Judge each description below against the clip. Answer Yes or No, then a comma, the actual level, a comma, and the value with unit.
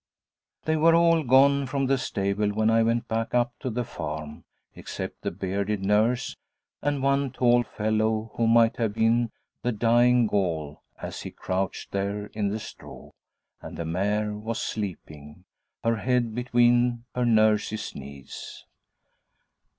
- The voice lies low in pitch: Yes, low, 115 Hz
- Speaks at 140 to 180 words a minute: Yes, average, 145 wpm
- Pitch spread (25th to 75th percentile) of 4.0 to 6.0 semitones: No, average, 3.1 semitones